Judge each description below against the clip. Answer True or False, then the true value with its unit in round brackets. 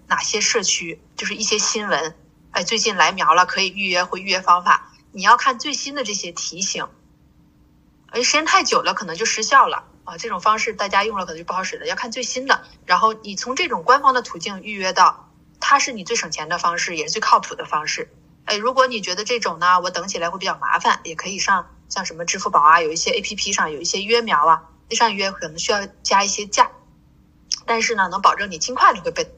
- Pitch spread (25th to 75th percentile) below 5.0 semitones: False (5.5 semitones)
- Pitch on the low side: False (210 Hz)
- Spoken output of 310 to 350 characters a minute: True (335 characters per minute)